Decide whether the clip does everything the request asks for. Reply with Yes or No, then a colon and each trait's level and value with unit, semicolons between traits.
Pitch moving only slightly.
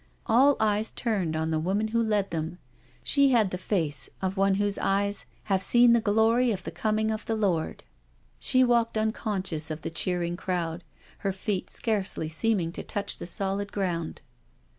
No: average, 3.8 semitones